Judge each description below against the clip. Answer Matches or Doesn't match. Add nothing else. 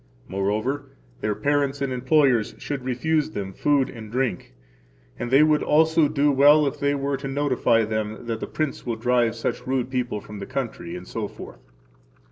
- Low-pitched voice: Matches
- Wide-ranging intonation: Doesn't match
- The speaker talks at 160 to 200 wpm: Matches